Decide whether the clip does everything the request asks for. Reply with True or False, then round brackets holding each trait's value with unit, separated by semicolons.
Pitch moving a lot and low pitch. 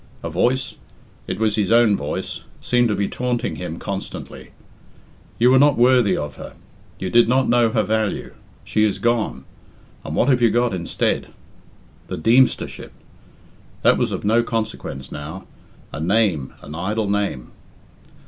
False (4.4 semitones; 110 Hz)